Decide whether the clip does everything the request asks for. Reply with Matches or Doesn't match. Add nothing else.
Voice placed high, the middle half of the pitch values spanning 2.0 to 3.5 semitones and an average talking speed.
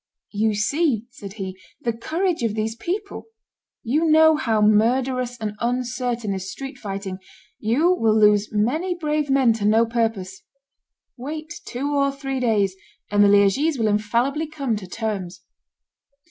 Doesn't match